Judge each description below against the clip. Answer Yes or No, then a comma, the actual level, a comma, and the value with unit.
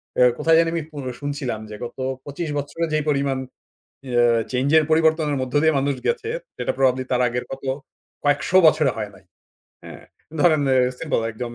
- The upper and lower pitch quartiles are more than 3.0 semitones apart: Yes, average, 3.7 semitones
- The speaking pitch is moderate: Yes, medium, 145 Hz